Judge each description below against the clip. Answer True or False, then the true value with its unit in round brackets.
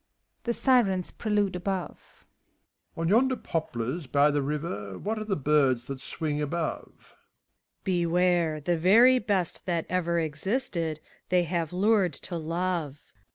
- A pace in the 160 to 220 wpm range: False (145 wpm)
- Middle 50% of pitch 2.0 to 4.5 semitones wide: True (4.1 semitones)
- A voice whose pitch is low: False (170 Hz)